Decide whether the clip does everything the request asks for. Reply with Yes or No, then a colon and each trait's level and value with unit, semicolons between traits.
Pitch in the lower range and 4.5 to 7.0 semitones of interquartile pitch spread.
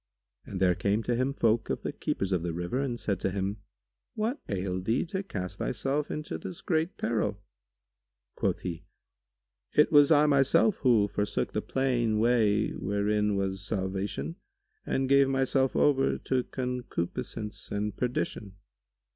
Yes: low, 110 Hz; average, 5.3 semitones